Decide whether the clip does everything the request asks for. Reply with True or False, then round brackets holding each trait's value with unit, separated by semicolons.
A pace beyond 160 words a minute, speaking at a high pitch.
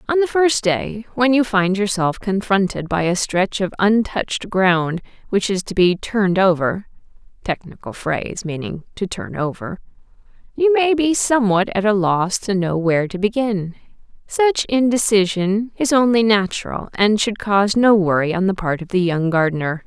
True (170 wpm; 200 Hz)